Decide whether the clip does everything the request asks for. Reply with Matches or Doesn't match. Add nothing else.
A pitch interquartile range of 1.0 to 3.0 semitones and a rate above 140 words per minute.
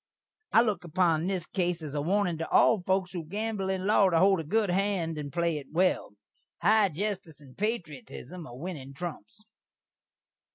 Doesn't match